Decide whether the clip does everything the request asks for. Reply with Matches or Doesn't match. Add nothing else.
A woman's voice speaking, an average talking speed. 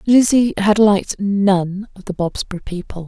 Matches